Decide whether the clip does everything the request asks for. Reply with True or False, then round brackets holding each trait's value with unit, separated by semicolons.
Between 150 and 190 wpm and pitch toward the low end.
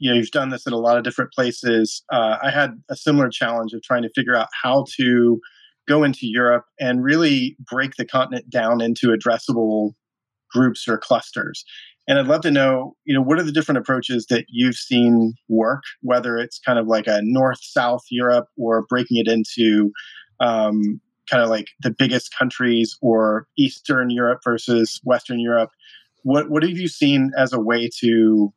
True (185 wpm; 120 Hz)